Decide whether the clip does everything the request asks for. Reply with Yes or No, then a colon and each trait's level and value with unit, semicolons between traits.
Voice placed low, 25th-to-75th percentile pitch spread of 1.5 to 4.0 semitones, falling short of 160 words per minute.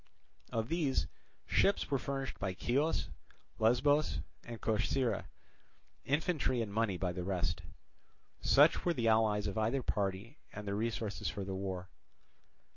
No: low, 110 Hz; average, 5.2 semitones; slow, 135 wpm